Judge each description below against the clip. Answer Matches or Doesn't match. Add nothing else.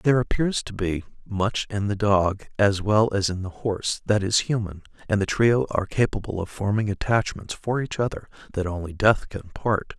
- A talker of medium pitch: Doesn't match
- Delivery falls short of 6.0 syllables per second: Matches